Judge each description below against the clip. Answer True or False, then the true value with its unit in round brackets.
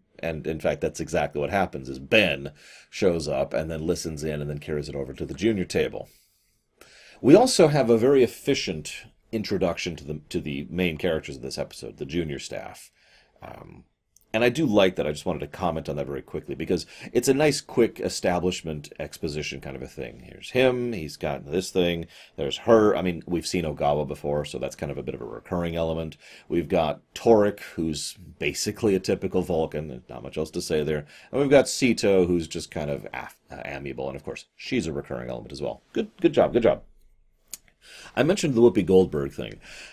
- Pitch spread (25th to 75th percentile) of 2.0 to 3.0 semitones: False (4.4 semitones)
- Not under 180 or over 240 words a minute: True (205 wpm)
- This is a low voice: True (80 Hz)